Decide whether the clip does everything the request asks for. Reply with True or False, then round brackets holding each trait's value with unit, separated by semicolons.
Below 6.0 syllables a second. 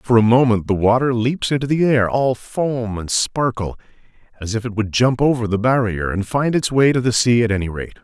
True (5.2 syllables/s)